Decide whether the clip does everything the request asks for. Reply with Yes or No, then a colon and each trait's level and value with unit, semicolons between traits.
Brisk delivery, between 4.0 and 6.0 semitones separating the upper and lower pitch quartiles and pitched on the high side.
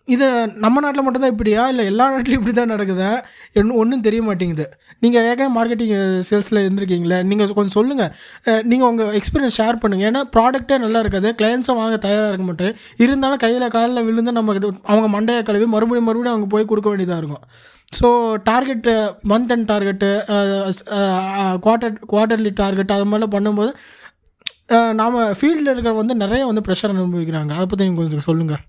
No: fast, 155 wpm; average, 2.8 semitones; high, 220 Hz